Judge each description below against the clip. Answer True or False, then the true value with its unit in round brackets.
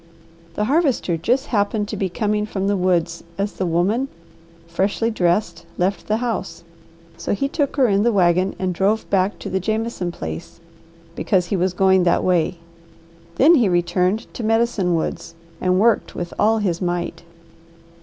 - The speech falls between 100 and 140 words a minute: False (165 wpm)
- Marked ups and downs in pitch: False (3.8 semitones)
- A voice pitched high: True (195 Hz)